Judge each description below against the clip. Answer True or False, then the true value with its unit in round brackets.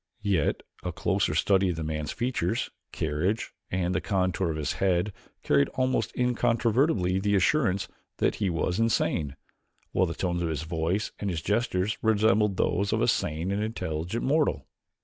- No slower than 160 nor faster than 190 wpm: True (165 wpm)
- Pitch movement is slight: False (4.7 semitones)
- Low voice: True (95 Hz)